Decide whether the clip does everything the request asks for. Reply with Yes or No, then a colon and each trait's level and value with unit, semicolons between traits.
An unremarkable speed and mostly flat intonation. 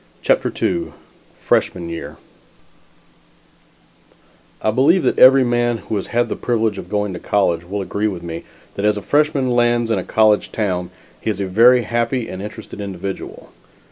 No: average, 170 wpm; average, 3.7 semitones